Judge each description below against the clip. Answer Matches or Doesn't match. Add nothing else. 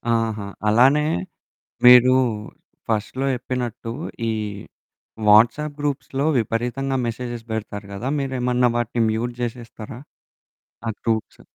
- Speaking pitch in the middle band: Doesn't match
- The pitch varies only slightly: Matches